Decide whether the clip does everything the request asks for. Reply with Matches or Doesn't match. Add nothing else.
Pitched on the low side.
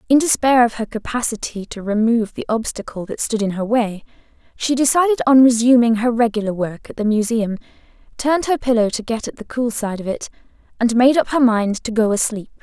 Doesn't match